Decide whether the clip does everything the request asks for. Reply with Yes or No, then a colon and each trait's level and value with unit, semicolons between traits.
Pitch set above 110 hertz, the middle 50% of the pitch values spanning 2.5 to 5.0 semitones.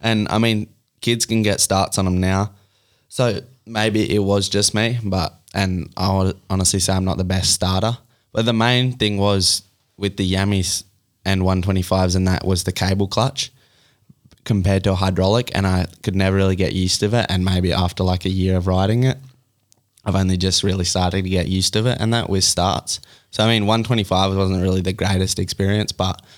No: low, 100 Hz; average, 2.9 semitones